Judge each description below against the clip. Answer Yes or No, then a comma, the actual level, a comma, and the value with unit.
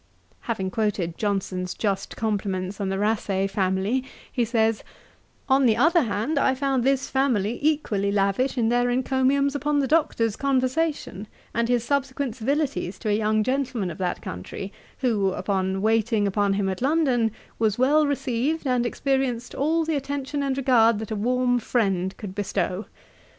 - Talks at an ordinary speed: Yes, average, 160 wpm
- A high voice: Yes, high, 230 Hz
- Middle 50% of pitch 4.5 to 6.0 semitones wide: Yes, average, 5.0 semitones